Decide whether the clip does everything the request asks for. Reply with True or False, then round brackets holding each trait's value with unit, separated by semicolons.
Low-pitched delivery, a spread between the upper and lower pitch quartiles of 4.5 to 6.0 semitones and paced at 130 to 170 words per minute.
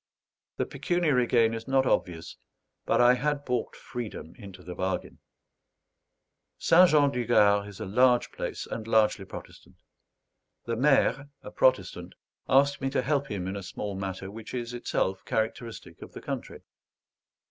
True (115 Hz; 4.9 semitones; 155 wpm)